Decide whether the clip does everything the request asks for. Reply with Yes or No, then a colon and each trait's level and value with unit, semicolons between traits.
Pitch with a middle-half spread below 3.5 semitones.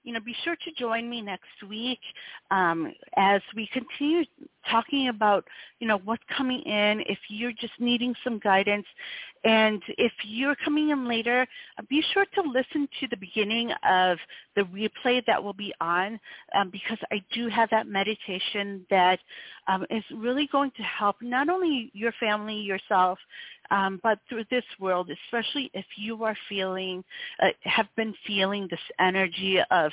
No: average, 4.1 semitones